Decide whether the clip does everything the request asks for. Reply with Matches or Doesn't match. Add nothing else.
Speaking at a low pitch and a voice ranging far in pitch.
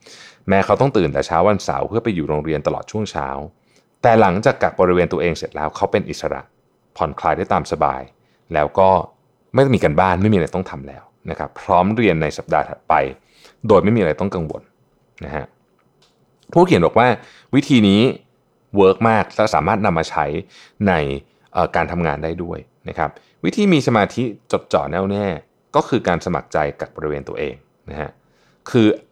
Matches